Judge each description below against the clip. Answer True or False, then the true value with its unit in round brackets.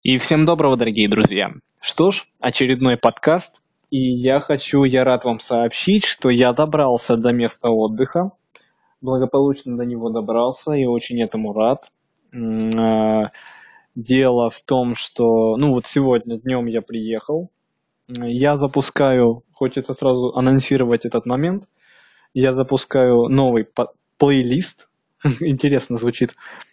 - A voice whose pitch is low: True (125 Hz)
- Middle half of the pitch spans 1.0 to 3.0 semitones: True (2.7 semitones)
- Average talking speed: True (120 wpm)